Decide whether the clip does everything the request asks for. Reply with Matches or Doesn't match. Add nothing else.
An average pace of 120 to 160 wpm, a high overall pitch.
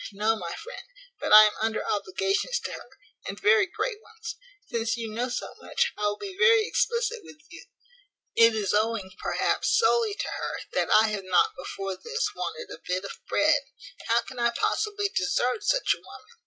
Doesn't match